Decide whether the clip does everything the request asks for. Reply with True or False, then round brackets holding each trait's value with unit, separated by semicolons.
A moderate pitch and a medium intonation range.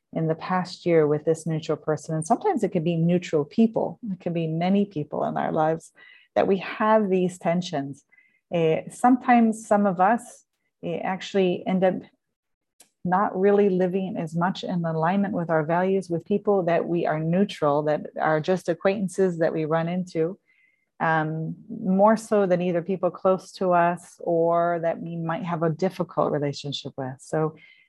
True (180 Hz; 3.4 semitones)